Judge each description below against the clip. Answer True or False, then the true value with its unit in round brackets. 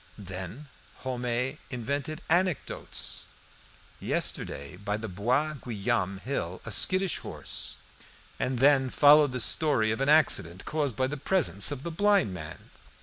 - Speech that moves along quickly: False (140 wpm)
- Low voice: True (130 Hz)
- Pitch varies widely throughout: True (6.5 semitones)